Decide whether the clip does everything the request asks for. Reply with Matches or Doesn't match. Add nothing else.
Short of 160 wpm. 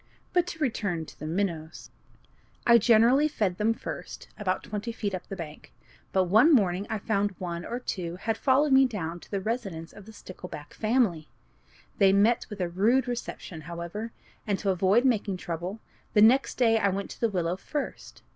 Doesn't match